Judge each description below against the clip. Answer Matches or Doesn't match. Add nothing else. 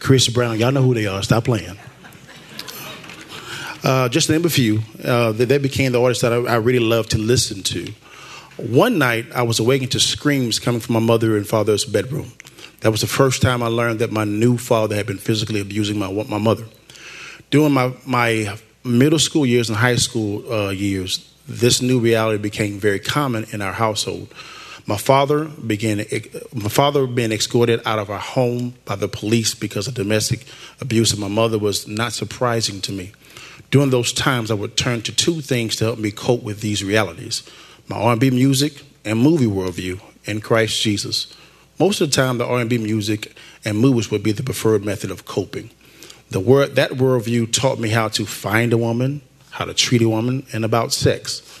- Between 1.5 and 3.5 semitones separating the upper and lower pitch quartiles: Matches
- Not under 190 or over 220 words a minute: Matches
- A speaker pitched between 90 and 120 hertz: Matches